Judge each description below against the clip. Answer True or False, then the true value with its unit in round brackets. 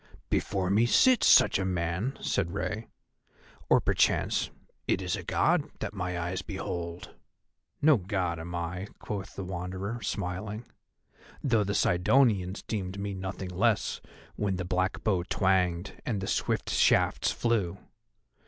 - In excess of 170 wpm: False (140 wpm)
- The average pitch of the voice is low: True (95 Hz)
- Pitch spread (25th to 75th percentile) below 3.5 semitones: True (2.6 semitones)